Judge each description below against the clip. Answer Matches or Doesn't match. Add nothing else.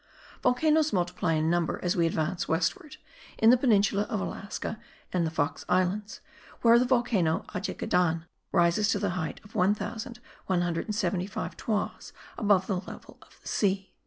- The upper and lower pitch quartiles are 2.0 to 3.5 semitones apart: Doesn't match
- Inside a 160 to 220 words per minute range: Doesn't match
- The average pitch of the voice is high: Matches